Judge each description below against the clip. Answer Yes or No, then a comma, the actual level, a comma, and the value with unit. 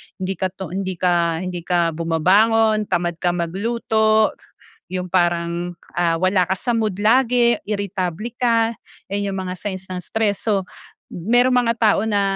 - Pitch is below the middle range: No, high, 190 Hz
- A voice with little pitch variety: No, average, 3.6 semitones